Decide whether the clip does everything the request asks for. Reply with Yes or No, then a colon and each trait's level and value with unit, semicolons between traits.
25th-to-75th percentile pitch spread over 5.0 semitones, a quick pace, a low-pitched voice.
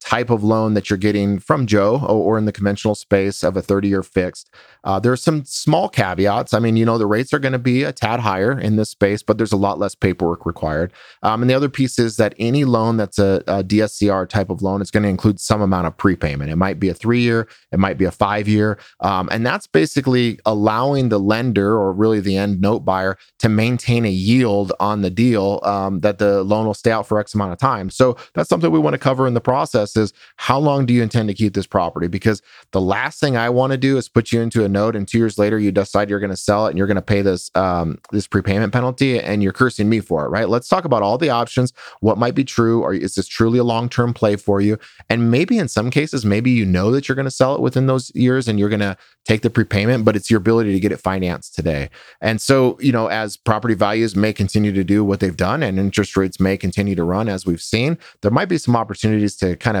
No: average, 3.2 semitones; fast, 260 wpm; low, 105 Hz